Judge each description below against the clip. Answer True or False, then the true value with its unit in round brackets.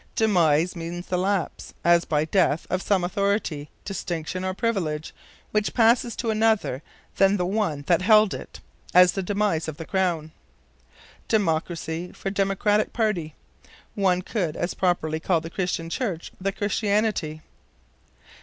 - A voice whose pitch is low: False (185 Hz)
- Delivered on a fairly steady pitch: False (3.7 semitones)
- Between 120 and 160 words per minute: True (140 wpm)